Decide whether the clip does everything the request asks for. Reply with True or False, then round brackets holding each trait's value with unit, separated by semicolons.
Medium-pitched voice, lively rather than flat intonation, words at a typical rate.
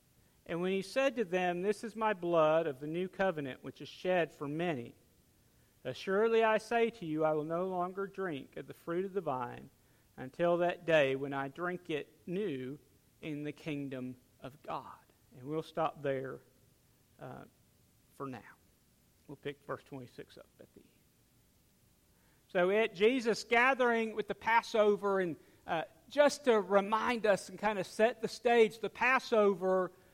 True (180 Hz; 6.4 semitones; 165 wpm)